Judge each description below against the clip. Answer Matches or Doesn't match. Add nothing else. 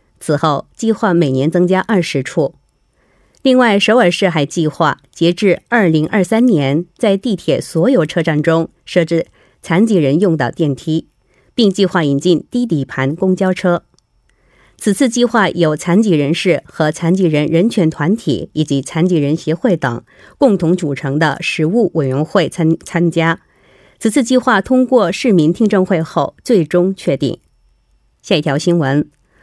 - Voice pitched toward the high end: Doesn't match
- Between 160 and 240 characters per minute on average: Matches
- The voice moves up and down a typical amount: Matches